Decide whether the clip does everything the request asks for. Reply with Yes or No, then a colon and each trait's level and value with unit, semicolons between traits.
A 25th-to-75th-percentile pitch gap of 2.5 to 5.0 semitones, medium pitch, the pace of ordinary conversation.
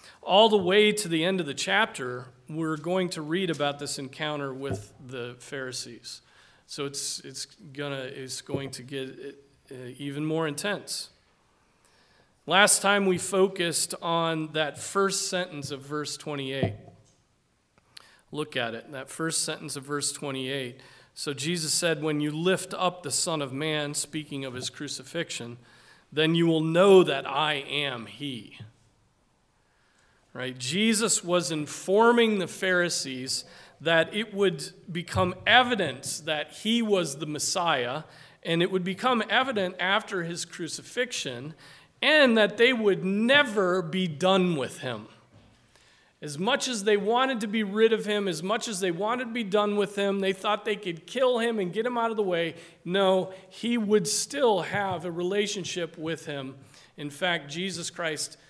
No: wide, 5.6 semitones; medium, 165 Hz; average, 155 wpm